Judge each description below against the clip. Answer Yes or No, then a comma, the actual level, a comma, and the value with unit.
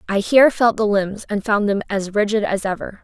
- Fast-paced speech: Yes, fast, 235 wpm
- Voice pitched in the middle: No, high, 210 Hz